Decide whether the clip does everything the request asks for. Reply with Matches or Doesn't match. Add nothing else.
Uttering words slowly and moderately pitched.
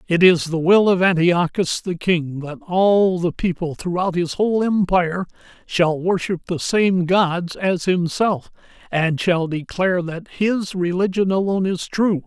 Doesn't match